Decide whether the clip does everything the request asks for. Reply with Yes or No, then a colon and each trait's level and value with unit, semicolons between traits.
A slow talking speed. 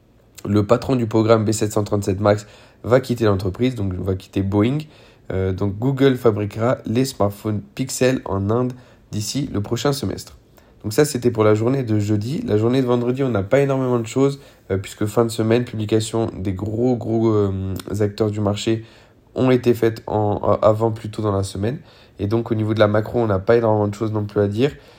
No: average, 200 wpm